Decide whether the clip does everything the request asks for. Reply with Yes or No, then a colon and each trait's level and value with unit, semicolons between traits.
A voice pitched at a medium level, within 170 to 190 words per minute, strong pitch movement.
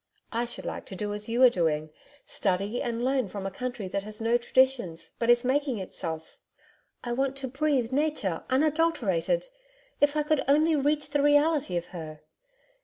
No: high, 240 Hz; average, 180 wpm; wide, 6.7 semitones